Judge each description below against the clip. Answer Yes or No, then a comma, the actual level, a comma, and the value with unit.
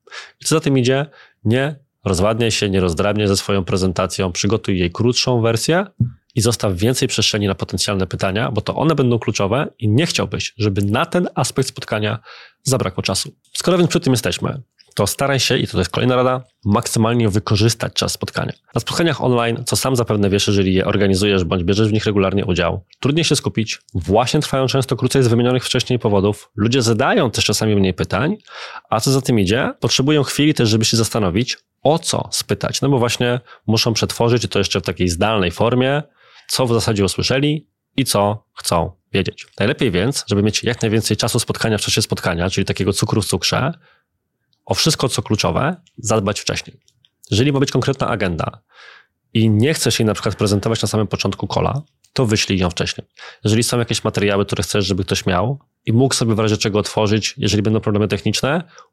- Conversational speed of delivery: No, fast, 185 wpm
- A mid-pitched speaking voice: No, low, 115 Hz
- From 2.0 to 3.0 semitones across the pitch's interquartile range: No, average, 4.2 semitones